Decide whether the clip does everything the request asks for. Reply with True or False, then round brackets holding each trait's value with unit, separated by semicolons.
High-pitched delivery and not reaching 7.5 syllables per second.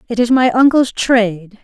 True (235 Hz; 4.9 syllables/s)